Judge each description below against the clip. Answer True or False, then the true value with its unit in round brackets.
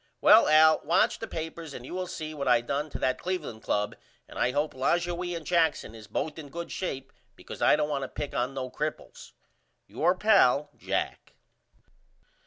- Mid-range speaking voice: True (150 Hz)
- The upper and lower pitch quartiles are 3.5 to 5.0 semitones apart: True (4.3 semitones)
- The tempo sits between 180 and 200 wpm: True (190 wpm)